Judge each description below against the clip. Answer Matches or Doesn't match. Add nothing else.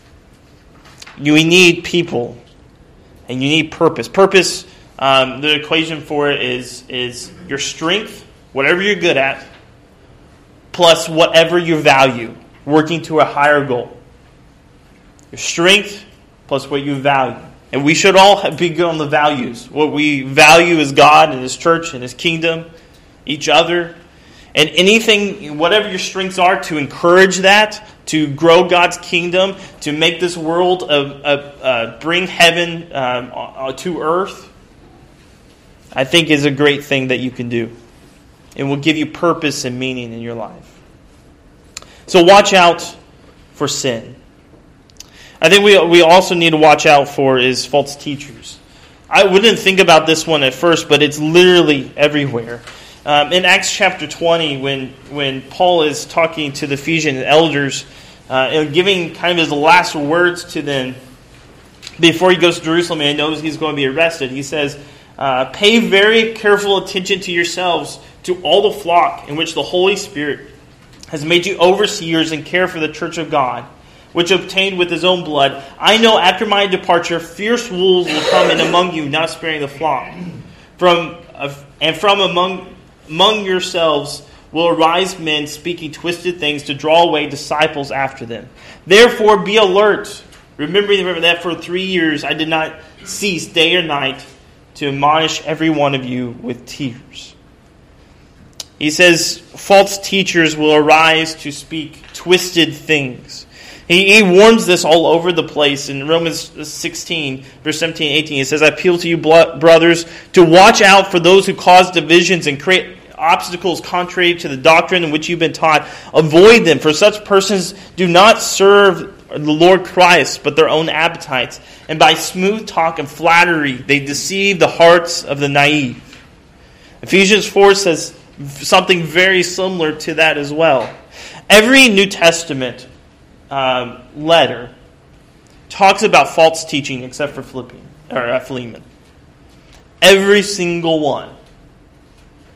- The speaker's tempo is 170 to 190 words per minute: Doesn't match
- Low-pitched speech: Doesn't match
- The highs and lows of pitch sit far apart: Doesn't match